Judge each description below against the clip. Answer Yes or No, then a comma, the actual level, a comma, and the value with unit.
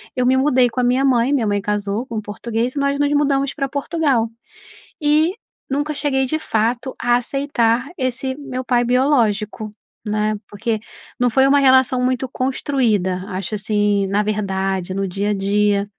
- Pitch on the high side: Yes, high, 245 Hz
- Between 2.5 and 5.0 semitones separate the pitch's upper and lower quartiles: Yes, average, 4.5 semitones